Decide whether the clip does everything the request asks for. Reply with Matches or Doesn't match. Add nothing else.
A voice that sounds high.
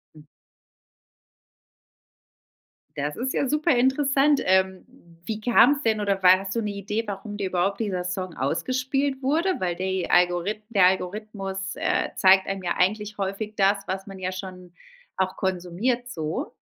Matches